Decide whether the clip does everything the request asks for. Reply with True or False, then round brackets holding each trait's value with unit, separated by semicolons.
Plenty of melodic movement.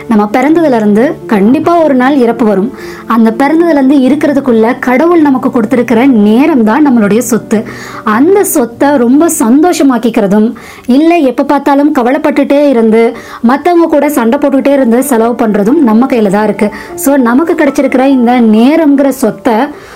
False (4.0 semitones)